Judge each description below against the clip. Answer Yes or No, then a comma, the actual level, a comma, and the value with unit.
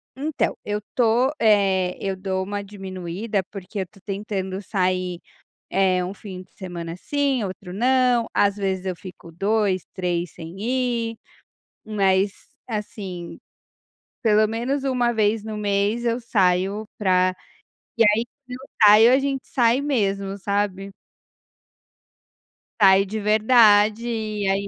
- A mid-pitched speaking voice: No, high, 205 Hz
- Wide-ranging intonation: No, average, 3.3 semitones